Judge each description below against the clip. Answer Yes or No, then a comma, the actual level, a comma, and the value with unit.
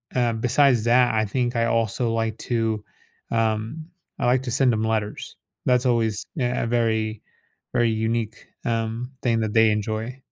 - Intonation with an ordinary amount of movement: No, narrow, 1.7 semitones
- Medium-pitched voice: No, low, 115 Hz